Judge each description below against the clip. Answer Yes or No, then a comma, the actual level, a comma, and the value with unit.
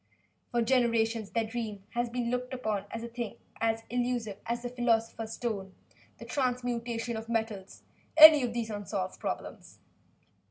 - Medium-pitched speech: No, high, 235 Hz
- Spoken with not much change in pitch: Yes, narrow, 1.7 semitones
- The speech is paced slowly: No, average, 145 wpm